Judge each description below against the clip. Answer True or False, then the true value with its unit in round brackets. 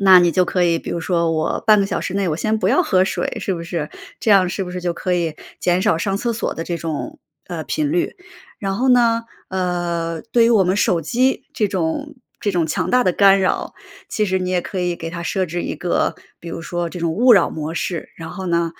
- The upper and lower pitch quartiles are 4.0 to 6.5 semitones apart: False (3.2 semitones)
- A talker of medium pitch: True (180 Hz)